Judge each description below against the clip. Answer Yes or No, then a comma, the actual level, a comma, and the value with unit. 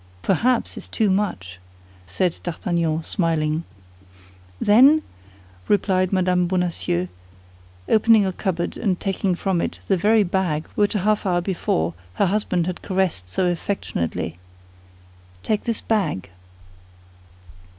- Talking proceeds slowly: Yes, slow, 120 wpm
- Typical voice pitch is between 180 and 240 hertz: Yes, medium, 185 Hz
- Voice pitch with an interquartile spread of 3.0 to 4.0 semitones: Yes, average, 3.7 semitones